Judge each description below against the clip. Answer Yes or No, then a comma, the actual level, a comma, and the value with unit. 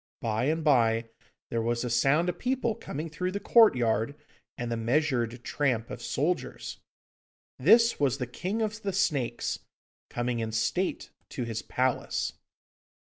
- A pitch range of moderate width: No, wide, 7.2 semitones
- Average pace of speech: Yes, average, 145 wpm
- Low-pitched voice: Yes, low, 130 Hz